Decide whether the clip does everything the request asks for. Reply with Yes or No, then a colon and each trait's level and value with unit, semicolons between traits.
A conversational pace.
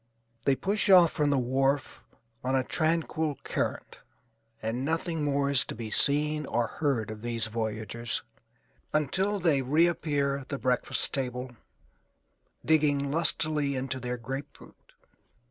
No: slow, 130 wpm